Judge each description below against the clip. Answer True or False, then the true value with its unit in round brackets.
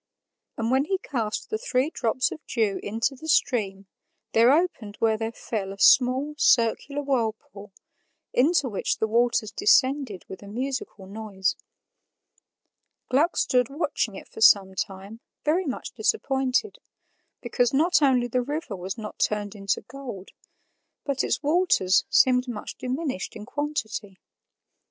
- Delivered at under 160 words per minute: True (140 wpm)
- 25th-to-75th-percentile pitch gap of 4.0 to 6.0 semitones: True (4.9 semitones)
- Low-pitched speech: False (245 Hz)